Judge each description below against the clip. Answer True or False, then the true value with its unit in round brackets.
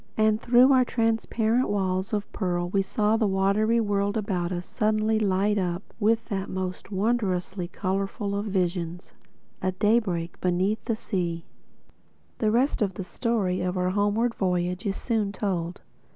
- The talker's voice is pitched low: False (200 Hz)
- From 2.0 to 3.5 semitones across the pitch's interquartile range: True (2.9 semitones)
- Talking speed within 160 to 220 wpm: False (150 wpm)